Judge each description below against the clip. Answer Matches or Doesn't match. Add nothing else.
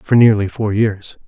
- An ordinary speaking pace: Matches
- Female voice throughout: Doesn't match